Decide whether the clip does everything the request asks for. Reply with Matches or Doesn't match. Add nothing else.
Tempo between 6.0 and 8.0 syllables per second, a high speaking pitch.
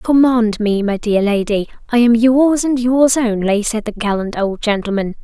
Doesn't match